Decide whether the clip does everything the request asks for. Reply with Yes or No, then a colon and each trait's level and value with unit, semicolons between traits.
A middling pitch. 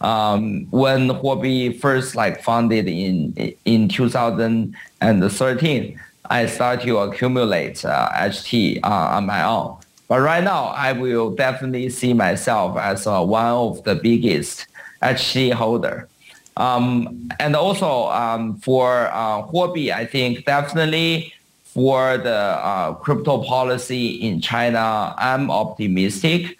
No: low, 125 Hz